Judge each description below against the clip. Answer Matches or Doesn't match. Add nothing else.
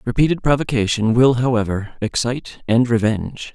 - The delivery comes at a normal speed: Doesn't match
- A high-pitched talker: Doesn't match